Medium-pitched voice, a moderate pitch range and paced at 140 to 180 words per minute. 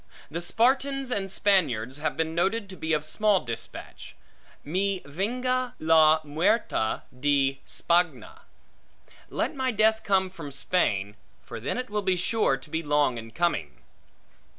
No: medium, 170 Hz; wide, 6.4 semitones; average, 145 wpm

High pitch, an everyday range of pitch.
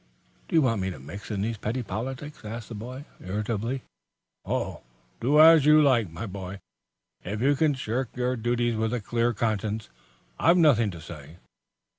No: low, 115 Hz; average, 4.1 semitones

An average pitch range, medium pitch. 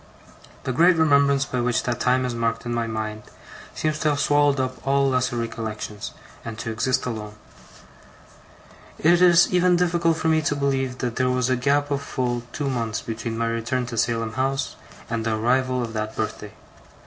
No: average, 3.6 semitones; low, 125 Hz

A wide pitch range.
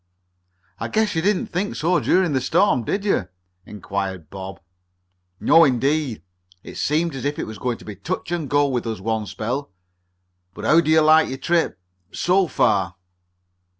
Yes: wide, 7.4 semitones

